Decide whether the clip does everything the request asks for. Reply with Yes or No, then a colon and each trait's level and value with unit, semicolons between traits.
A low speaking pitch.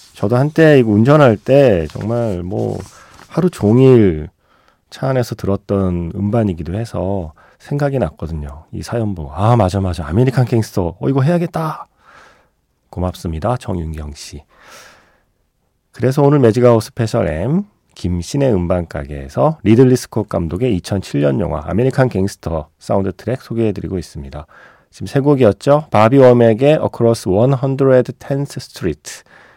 Yes: low, 110 Hz